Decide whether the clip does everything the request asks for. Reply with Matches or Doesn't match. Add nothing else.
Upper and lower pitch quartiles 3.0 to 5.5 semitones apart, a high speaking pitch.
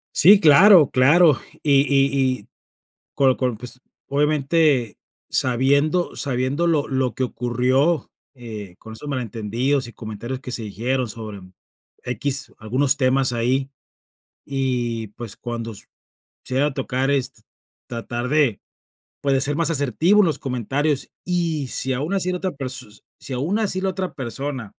Doesn't match